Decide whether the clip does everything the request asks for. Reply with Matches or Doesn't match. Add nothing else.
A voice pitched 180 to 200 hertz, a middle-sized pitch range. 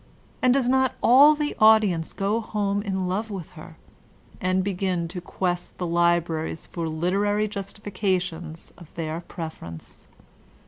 Matches